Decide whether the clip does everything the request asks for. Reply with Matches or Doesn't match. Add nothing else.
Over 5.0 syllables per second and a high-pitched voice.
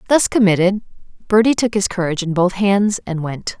Matches